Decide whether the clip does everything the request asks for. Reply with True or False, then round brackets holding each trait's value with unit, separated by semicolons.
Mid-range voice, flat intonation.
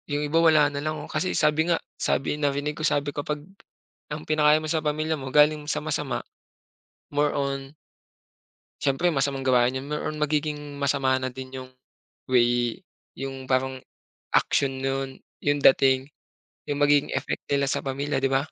True (145 Hz; 2.0 semitones)